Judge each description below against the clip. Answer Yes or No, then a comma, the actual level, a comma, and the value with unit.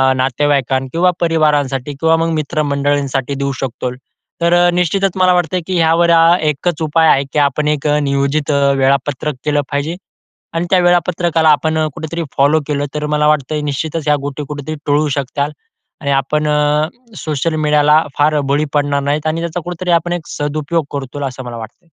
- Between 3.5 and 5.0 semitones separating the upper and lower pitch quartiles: No, narrow, 2.5 semitones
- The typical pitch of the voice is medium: Yes, medium, 150 Hz